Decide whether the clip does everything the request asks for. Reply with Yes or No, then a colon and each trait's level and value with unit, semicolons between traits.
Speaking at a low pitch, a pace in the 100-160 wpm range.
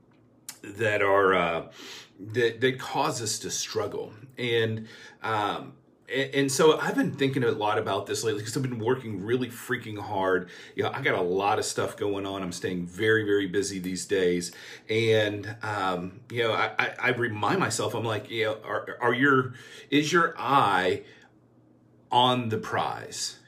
No: low, 110 Hz; average, 175 wpm